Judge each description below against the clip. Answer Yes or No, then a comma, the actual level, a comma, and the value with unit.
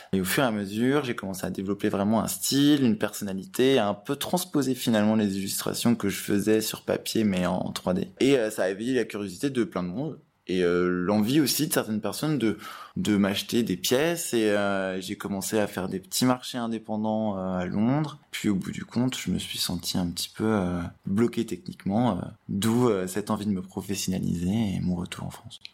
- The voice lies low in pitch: Yes, low, 105 Hz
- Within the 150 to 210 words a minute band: No, fast, 220 wpm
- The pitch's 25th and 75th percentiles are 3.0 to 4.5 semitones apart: Yes, average, 3.7 semitones